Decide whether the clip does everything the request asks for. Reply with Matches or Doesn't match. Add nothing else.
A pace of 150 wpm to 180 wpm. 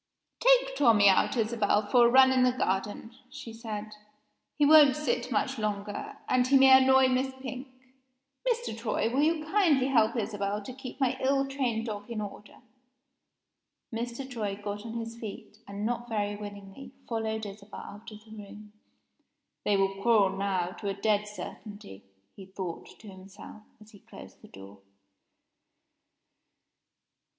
Matches